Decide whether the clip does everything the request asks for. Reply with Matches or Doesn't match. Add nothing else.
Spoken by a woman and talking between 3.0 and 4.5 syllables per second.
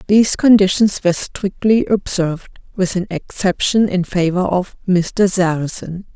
Matches